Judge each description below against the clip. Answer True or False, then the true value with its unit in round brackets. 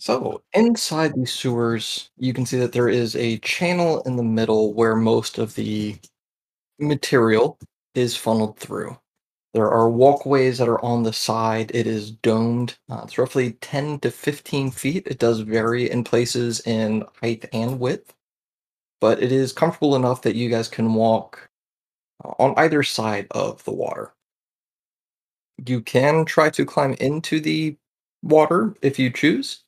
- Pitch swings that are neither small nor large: True (4.3 semitones)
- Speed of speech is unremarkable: True (155 wpm)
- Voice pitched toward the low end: True (125 Hz)